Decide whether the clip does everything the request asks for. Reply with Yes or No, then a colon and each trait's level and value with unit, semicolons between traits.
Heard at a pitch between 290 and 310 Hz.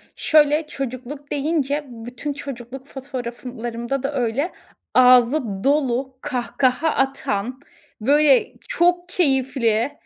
No: very high, 265 Hz